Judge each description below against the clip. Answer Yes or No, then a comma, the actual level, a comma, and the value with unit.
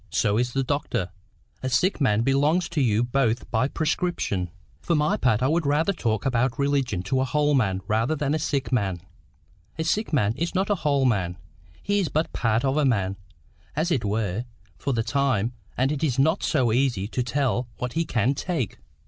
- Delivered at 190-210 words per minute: Yes, average, 200 wpm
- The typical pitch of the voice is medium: No, low, 130 Hz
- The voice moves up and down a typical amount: Yes, average, 4.8 semitones